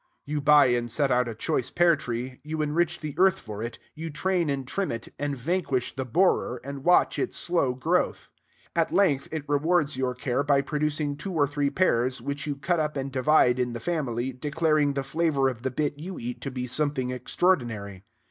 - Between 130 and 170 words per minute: No, fast, 205 wpm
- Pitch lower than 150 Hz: Yes, medium, 140 Hz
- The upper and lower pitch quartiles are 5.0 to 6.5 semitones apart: No, average, 3.7 semitones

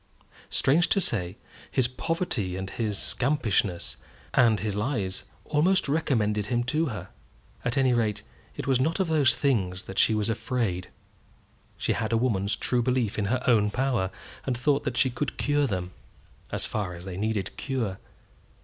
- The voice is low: Yes, low, 120 Hz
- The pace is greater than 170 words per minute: No, average, 165 wpm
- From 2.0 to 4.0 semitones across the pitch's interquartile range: No, average, 4.9 semitones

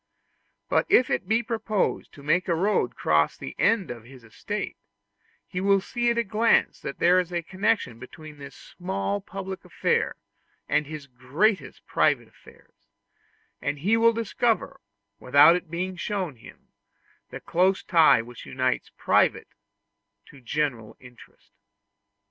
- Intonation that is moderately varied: No, wide, 7.4 semitones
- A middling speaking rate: Yes, average, 150 wpm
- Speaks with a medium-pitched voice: Yes, medium, 170 Hz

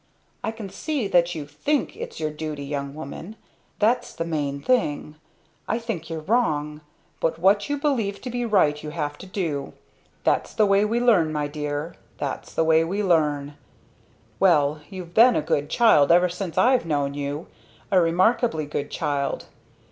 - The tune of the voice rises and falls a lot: Yes, wide, 6.2 semitones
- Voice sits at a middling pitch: Yes, medium, 165 Hz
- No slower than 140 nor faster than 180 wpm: Yes, average, 170 wpm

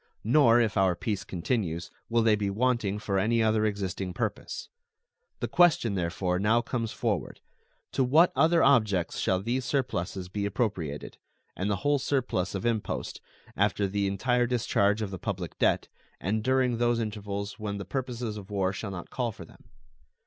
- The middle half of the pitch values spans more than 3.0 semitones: Yes, average, 3.6 semitones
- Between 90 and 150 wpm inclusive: No, average, 170 wpm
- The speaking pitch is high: No, low, 105 Hz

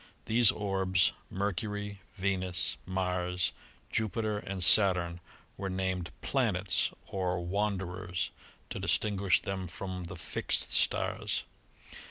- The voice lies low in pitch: Yes, very low, 95 Hz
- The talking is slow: Yes, slow, 105 wpm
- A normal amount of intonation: No, narrow, 2.0 semitones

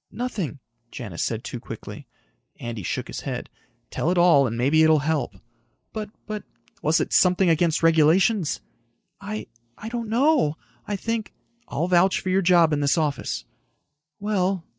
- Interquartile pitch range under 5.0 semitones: No, average, 5.3 semitones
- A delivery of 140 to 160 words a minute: Yes, average, 155 wpm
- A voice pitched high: No, medium, 175 Hz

